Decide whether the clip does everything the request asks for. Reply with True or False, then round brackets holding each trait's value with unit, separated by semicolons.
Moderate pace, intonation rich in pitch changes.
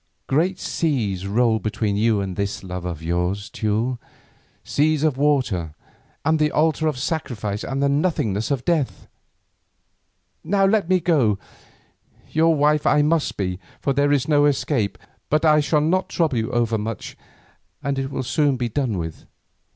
True (160 wpm; 6.4 semitones)